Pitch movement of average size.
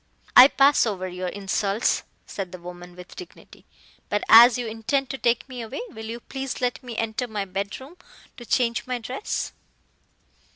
Yes: average, 4.2 semitones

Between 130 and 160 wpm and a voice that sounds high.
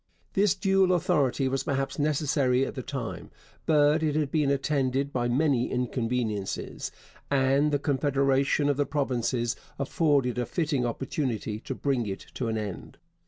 No: average, 150 wpm; low, 135 Hz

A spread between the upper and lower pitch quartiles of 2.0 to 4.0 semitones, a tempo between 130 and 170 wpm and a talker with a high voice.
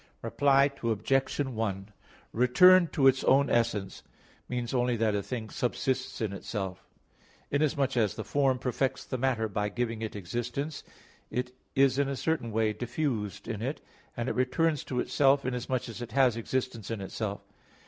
No: average, 3.3 semitones; average, 160 wpm; low, 125 Hz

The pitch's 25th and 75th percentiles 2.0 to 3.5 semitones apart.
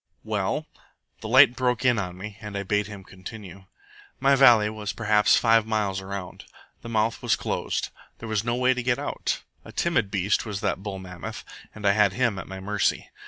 Yes: average, 3.0 semitones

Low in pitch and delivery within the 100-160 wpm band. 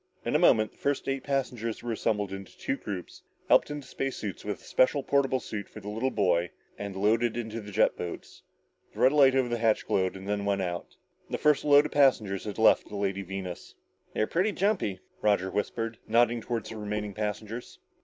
No: low, 110 Hz; fast, 205 wpm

